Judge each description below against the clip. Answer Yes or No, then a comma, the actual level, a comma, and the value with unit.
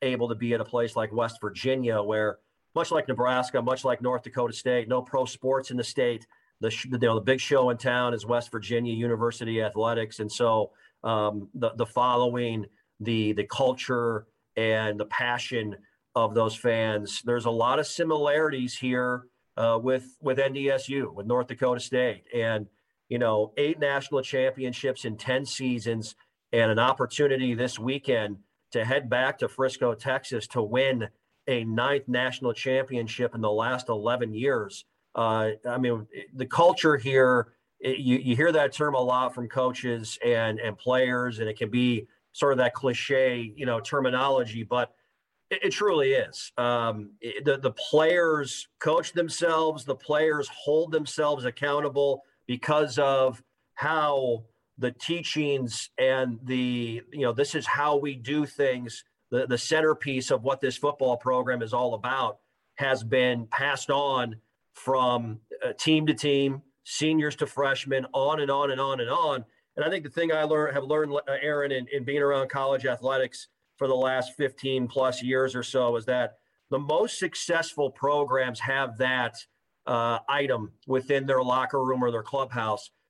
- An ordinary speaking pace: Yes, average, 165 wpm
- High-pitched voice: No, low, 125 Hz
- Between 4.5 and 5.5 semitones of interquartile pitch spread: No, average, 2.9 semitones